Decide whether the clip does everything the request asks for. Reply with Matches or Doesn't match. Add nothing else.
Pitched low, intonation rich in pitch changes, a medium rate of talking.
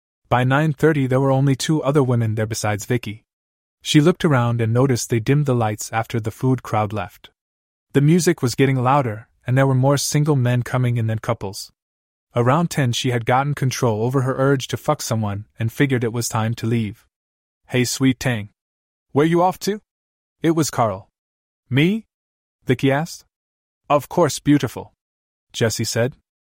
Doesn't match